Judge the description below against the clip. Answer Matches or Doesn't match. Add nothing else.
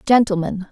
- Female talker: Matches